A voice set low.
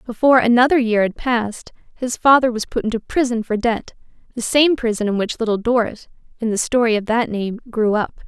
No: high, 230 Hz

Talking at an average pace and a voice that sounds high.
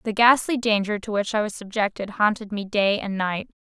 No: fast, 215 wpm; high, 210 Hz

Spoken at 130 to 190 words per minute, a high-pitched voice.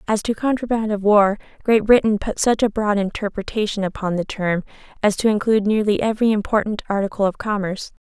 Yes: average, 180 wpm; high, 210 Hz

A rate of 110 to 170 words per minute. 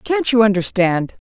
Yes: average, 140 wpm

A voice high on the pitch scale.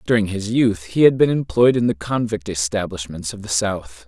No: low, 105 Hz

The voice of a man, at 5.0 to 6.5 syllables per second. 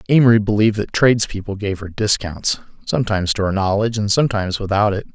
No: male; 6.9 syllables/s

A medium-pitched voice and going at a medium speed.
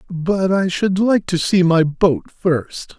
Yes: medium, 180 Hz; average, 180 wpm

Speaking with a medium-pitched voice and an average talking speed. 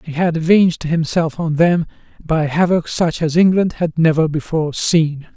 Yes: medium, 160 Hz; average, 170 wpm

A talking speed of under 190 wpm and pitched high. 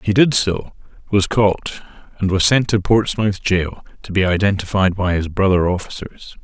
No: average, 170 wpm; very low, 95 Hz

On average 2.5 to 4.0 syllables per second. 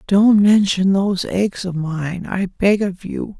Yes: 3.8 syllables/s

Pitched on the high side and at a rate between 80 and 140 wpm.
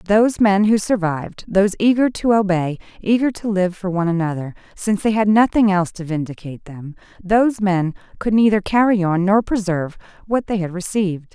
No: high, 195 Hz; average, 175 wpm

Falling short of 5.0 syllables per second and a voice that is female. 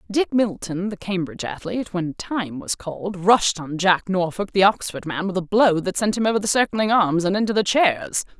No: 5.1 syllables/s; female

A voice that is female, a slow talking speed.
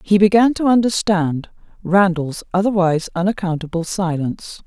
Yes: female; slow, 105 wpm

